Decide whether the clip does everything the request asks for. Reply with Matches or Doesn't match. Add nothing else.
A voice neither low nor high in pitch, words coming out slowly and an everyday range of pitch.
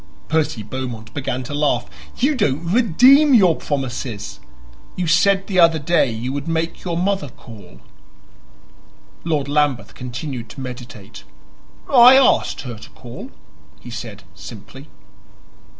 Doesn't match